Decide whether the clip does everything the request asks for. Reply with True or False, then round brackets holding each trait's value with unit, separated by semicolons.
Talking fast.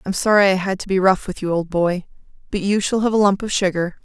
True (280 wpm)